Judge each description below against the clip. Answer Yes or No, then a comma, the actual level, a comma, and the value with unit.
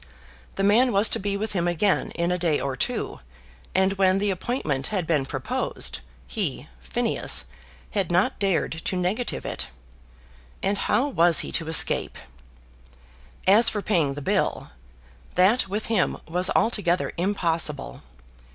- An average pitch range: Yes, average, 3.6 semitones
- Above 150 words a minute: No, average, 145 wpm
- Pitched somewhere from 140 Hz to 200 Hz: Yes, medium, 185 Hz